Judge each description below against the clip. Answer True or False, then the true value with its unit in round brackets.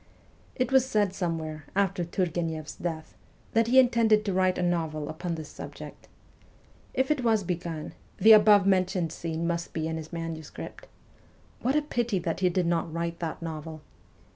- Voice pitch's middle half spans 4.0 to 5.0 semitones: True (4.3 semitones)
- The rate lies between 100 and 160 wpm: False (170 wpm)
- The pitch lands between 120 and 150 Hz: False (175 Hz)